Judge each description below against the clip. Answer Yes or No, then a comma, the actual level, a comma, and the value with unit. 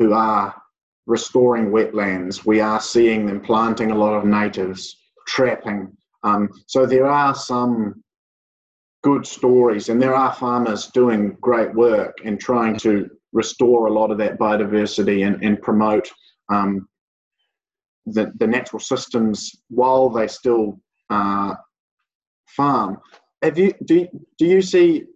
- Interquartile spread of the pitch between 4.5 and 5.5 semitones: No, average, 3.2 semitones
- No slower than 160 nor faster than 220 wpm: No, slow, 135 wpm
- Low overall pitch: Yes, low, 110 Hz